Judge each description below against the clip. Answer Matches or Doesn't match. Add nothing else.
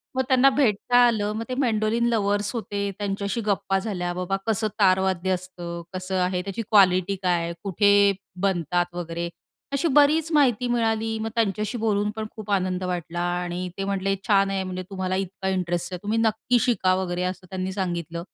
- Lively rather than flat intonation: Doesn't match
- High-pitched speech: Matches